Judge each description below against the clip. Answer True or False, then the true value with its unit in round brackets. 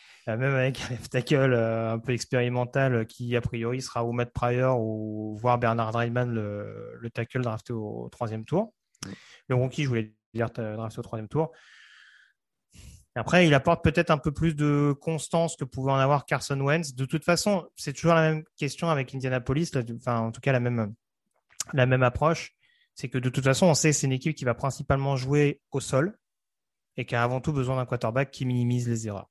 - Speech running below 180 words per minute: False (205 wpm)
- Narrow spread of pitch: False (3.8 semitones)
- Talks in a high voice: False (130 Hz)